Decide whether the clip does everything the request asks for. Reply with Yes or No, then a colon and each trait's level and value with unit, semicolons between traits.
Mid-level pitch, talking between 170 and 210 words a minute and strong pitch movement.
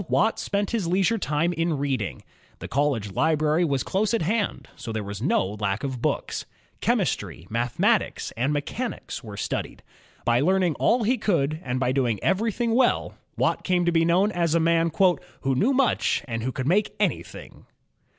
Yes: medium, 160 Hz; average, 175 wpm; wide, 7.1 semitones